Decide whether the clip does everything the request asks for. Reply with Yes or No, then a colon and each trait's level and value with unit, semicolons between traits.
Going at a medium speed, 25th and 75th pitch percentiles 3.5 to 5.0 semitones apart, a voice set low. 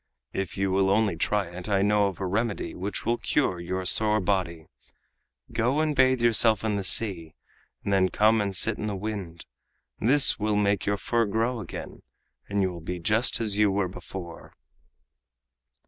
No: average, 180 wpm; average, 2.9 semitones; low, 100 Hz